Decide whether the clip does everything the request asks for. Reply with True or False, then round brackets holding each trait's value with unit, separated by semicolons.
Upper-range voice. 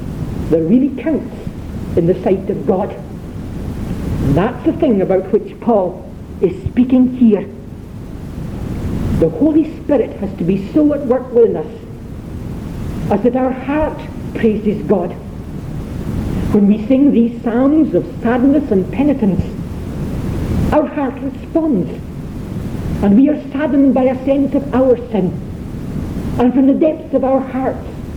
True (255 Hz)